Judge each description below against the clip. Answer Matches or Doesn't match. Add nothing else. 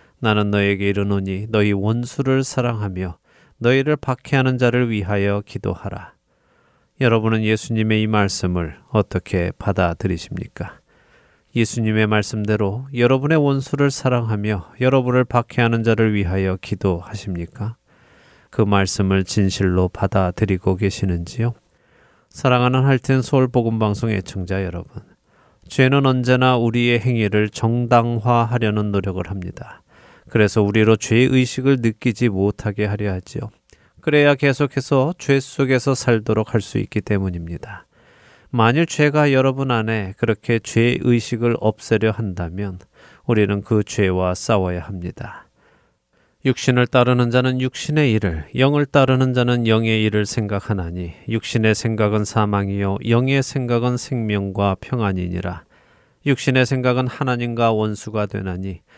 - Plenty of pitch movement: Doesn't match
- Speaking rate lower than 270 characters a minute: Doesn't match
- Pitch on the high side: Doesn't match